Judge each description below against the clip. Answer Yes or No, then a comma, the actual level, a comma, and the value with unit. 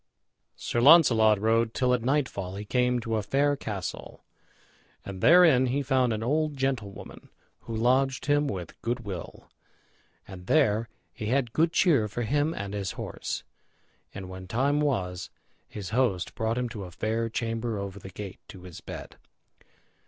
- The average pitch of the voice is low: Yes, low, 115 Hz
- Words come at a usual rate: Yes, average, 160 wpm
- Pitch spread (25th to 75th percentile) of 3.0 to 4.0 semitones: No, average, 4.9 semitones